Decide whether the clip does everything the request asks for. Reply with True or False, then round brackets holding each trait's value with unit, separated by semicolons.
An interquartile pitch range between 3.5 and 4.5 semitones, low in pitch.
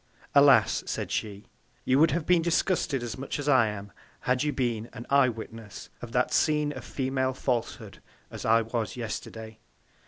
True (3.9 semitones; 125 Hz)